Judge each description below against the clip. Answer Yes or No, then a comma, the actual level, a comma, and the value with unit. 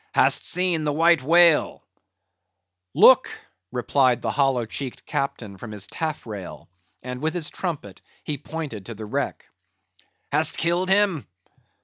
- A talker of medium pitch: Yes, medium, 145 Hz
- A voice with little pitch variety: No, wide, 5.4 semitones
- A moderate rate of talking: No, slow, 130 wpm